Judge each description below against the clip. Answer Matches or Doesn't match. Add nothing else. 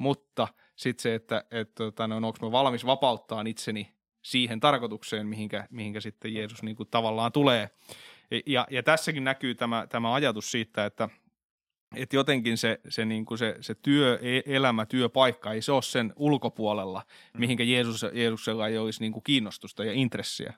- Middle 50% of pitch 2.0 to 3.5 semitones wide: Matches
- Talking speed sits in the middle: Doesn't match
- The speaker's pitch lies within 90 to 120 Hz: Matches